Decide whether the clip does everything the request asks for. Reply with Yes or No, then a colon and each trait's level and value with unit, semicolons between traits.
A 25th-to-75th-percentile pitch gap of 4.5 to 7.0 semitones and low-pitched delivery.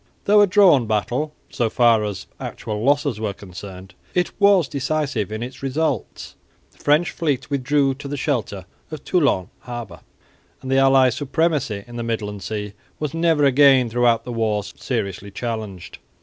Yes: average, 5.3 semitones; low, 125 Hz